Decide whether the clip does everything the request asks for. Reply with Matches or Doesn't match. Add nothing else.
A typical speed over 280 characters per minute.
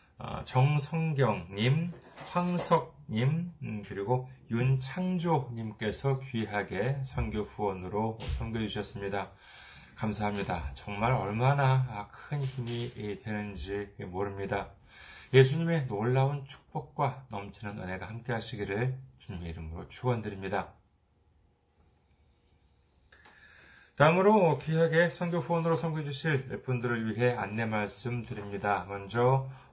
Doesn't match